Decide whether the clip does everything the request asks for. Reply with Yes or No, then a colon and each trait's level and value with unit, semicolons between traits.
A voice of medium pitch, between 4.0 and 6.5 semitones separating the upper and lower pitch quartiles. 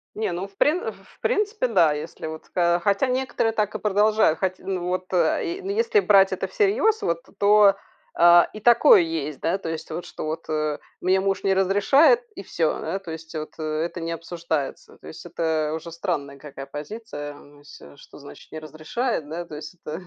Yes: medium, 175 Hz; average, 5.1 semitones